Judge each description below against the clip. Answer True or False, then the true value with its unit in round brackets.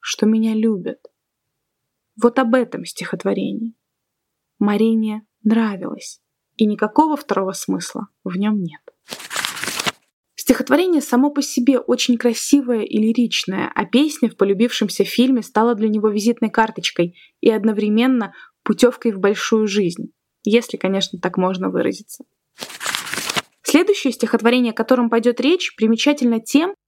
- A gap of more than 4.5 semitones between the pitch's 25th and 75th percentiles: False (3.1 semitones)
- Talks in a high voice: True (230 Hz)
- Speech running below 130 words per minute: True (120 wpm)